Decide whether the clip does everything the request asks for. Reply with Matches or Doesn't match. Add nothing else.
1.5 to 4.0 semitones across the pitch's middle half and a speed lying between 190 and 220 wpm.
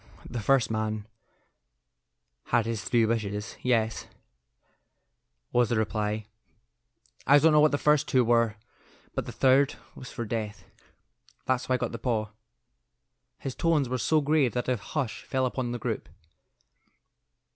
Doesn't match